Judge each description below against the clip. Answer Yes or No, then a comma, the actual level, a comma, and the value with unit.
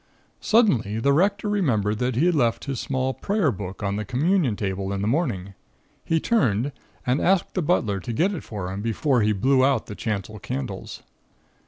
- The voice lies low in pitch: Yes, low, 125 Hz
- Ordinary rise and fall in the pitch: No, wide, 7.7 semitones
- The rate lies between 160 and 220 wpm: Yes, average, 190 wpm